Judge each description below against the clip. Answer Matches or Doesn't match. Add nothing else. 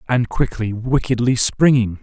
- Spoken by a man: Matches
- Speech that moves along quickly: Doesn't match